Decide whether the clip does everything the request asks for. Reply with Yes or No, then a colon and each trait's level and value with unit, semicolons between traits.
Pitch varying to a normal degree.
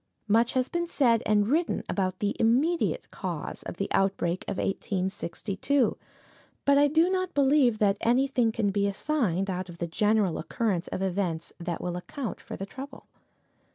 No: wide, 6.2 semitones